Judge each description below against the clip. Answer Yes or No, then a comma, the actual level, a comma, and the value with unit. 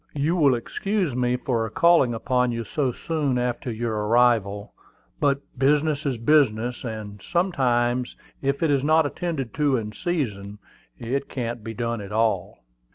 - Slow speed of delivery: No, average, 155 wpm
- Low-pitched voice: Yes, low, 125 Hz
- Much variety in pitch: No, average, 4.1 semitones